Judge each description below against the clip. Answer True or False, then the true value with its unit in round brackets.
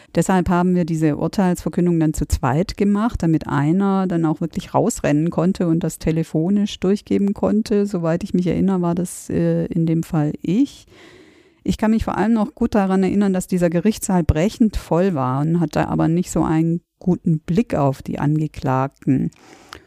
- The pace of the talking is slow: False (170 wpm)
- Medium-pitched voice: True (175 Hz)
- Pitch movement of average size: True (3.5 semitones)